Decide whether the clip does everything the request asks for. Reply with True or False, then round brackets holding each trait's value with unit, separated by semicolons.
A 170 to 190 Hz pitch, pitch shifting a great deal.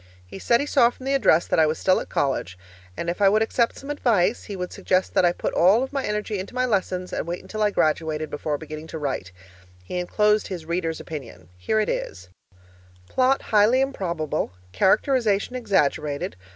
True (185 Hz; 5.9 semitones)